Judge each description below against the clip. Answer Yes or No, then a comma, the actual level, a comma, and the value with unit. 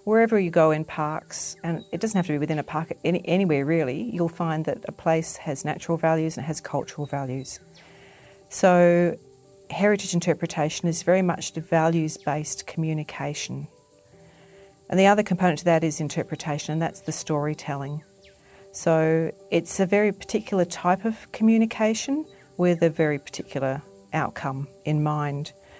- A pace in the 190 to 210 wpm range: No, average, 155 wpm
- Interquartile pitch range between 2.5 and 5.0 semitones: Yes, average, 3.7 semitones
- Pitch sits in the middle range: Yes, medium, 165 Hz